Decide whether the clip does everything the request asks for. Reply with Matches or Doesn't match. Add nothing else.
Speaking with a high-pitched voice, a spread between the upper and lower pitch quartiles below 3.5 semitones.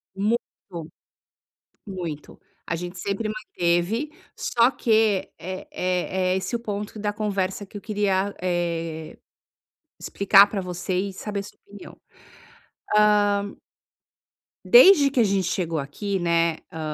Matches